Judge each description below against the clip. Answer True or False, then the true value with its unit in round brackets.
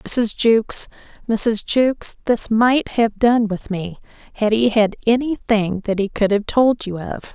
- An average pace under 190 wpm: True (180 wpm)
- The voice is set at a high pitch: True (220 Hz)